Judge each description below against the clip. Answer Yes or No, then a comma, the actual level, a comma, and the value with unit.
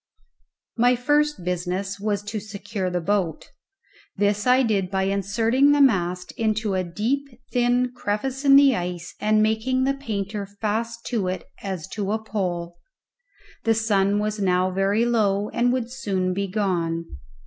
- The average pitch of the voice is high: Yes, high, 205 Hz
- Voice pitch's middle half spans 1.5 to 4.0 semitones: Yes, average, 3.6 semitones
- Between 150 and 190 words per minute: Yes, average, 155 wpm